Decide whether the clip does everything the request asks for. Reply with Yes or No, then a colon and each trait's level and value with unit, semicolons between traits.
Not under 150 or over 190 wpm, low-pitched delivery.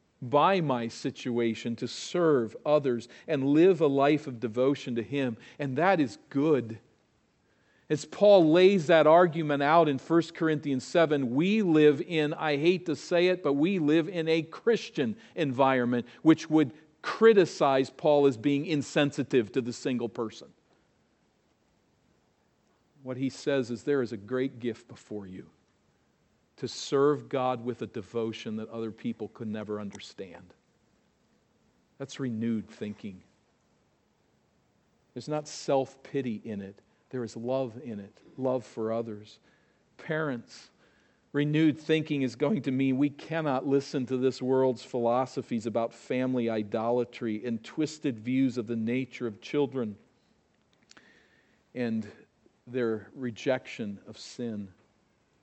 No: slow, 135 wpm; low, 130 Hz